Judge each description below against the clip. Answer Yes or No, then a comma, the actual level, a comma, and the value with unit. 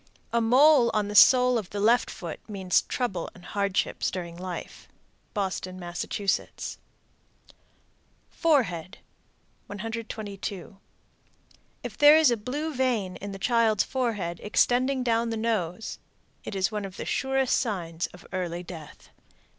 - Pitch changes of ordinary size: Yes, average, 4.8 semitones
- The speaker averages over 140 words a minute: No, slow, 135 wpm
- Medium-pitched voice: No, high, 210 Hz